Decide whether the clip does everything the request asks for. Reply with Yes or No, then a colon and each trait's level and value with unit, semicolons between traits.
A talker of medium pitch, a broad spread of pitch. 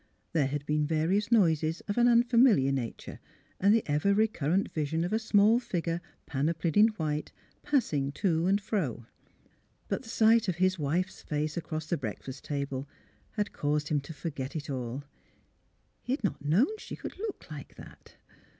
Yes: medium, 165 Hz; wide, 6.0 semitones